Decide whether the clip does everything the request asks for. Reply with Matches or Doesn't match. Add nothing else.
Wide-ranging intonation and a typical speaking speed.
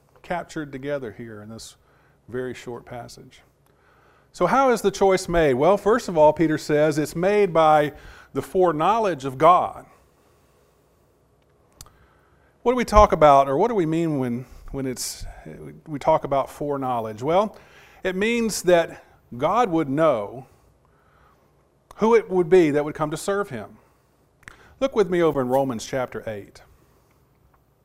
Matches